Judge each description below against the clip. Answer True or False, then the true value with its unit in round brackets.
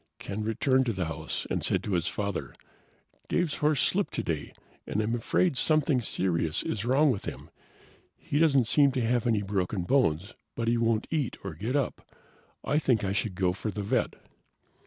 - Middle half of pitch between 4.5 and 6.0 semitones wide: True (5.5 semitones)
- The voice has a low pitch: True (115 Hz)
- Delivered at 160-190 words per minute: True (185 wpm)